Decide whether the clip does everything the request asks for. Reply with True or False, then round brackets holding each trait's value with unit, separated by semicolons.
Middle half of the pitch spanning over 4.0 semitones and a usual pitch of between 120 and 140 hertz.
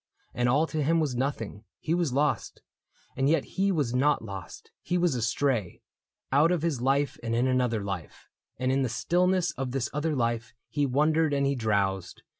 True (4.7 semitones; 135 Hz)